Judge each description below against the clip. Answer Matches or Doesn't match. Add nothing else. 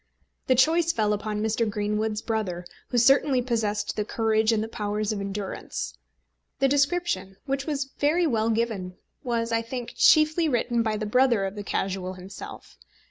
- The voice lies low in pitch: Doesn't match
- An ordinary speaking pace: Matches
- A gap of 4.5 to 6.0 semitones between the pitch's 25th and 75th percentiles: Doesn't match